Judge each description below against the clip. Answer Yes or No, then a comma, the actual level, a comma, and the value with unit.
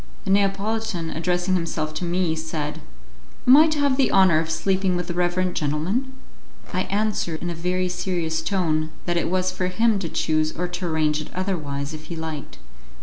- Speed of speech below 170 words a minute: No, average, 190 wpm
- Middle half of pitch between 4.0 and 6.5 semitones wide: No, average, 3.0 semitones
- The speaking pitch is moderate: Yes, medium, 175 Hz